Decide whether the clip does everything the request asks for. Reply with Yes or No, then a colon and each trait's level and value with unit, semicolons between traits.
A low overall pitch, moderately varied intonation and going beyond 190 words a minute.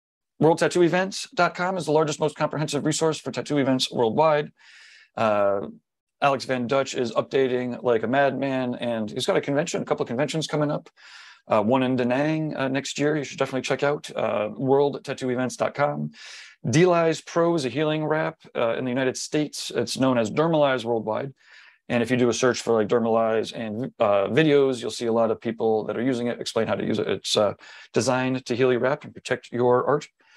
Yes: low, 130 Hz; average, 3.9 semitones; average, 200 wpm